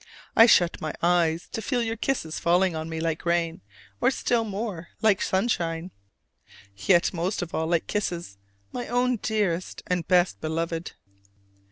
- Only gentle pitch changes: No, average, 4.6 semitones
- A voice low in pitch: No, medium, 175 Hz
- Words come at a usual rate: Yes, average, 155 wpm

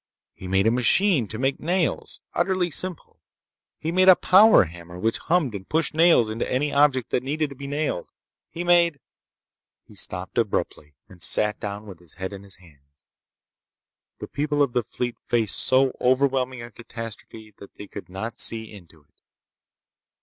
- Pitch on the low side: Yes, low, 120 Hz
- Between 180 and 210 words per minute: No, average, 170 wpm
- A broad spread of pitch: Yes, wide, 6.9 semitones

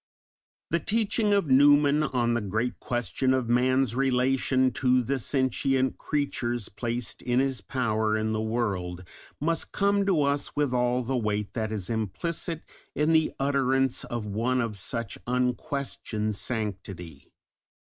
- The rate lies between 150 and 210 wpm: No, average, 140 wpm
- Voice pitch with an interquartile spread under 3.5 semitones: No, average, 3.9 semitones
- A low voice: Yes, low, 125 Hz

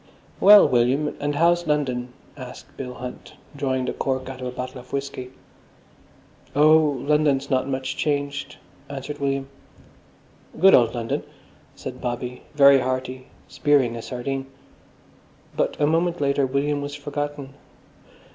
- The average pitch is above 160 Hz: No, low, 135 Hz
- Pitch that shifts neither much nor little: No, narrow, 2.3 semitones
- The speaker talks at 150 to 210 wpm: No, slow, 135 wpm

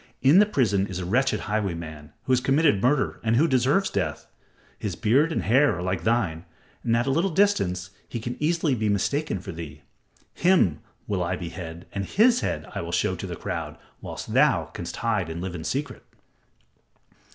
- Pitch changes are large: Yes, wide, 7.7 semitones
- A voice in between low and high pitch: No, low, 110 Hz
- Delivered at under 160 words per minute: No, average, 190 wpm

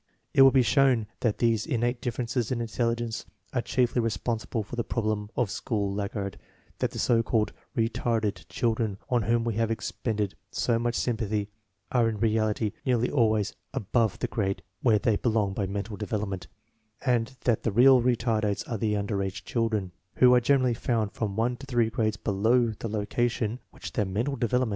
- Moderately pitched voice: No, low, 115 Hz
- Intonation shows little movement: Yes, narrow, 2.3 semitones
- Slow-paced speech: No, average, 185 wpm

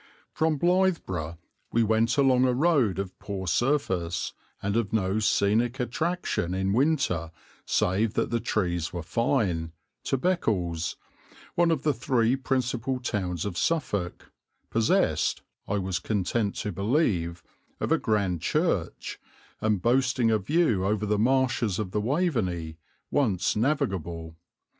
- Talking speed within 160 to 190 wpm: No, slow, 135 wpm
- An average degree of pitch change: No, wide, 6.0 semitones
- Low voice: Yes, low, 110 Hz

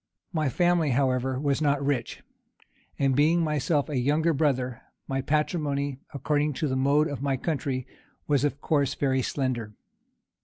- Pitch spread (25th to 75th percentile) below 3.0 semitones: Yes, narrow, 2.4 semitones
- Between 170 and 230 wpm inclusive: No, average, 150 wpm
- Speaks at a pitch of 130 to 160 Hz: Yes, medium, 140 Hz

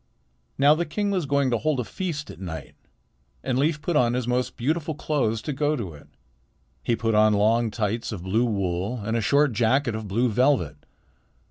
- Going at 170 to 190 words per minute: No, average, 200 wpm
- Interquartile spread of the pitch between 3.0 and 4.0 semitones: No, average, 5.2 semitones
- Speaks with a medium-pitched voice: No, low, 120 Hz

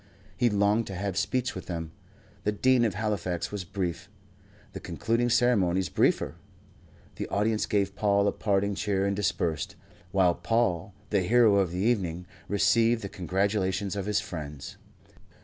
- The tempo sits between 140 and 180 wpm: Yes, average, 150 wpm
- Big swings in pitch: No, narrow, 2.5 semitones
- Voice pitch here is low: Yes, low, 100 Hz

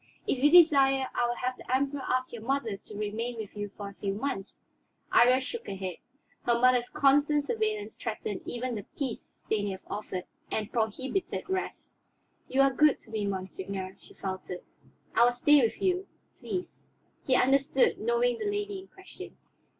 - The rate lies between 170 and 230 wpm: Yes, average, 175 wpm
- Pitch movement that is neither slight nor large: No, wide, 5.9 semitones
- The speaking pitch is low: No, very high, 255 Hz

